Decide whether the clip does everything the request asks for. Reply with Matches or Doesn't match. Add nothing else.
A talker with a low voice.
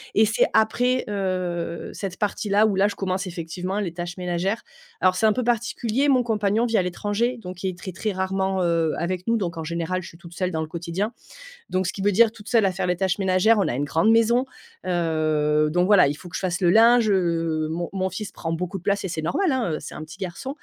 Doesn't match